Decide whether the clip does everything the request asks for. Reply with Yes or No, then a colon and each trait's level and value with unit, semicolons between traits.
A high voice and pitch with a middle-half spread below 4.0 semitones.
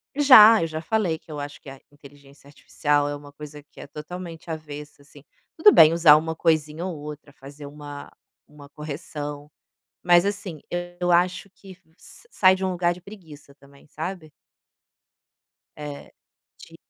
No: medium, 155 Hz; average, 3.5 semitones